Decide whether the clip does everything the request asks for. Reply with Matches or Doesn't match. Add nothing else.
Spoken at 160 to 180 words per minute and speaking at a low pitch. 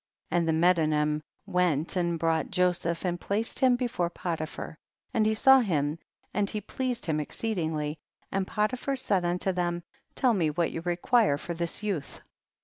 Doesn't match